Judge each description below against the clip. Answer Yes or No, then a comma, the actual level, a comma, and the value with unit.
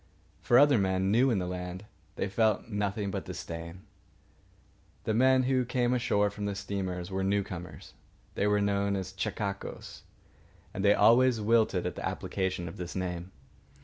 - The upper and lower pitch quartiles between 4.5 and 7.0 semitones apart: No, average, 3.0 semitones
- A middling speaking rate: Yes, average, 160 wpm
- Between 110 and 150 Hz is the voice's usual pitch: No, low, 100 Hz